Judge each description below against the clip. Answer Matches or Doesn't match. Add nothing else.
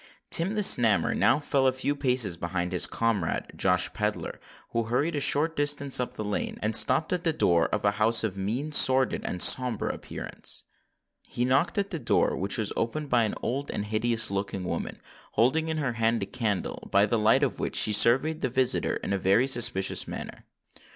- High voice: Doesn't match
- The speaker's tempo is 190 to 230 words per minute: Matches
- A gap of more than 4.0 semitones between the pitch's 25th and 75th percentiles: Matches